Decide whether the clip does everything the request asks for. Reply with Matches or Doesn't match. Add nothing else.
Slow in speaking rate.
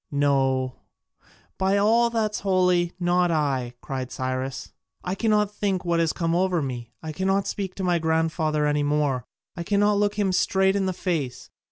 Doesn't match